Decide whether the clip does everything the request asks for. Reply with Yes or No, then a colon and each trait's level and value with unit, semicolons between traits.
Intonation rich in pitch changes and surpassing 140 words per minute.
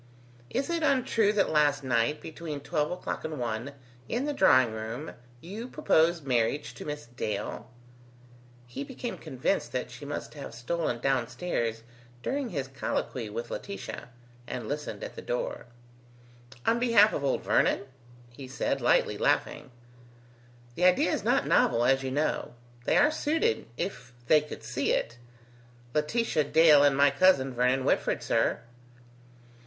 Yes: wide, 6.8 semitones; average, 150 wpm